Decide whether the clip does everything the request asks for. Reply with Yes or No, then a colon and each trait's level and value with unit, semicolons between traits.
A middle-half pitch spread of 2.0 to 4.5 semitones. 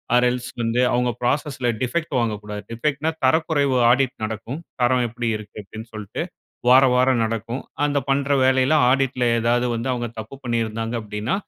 Yes: average, 2.7 semitones